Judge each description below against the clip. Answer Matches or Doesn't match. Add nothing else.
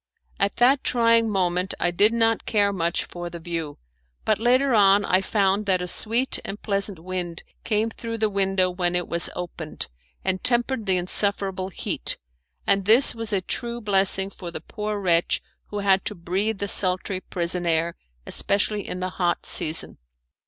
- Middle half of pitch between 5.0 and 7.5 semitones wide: Doesn't match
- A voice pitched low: Doesn't match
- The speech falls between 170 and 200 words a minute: Matches